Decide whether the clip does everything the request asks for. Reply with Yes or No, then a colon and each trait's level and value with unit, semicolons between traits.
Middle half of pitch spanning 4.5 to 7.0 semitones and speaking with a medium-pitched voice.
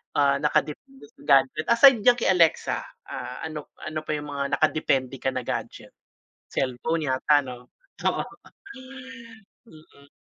No: average, 3.4 semitones; medium, 150 Hz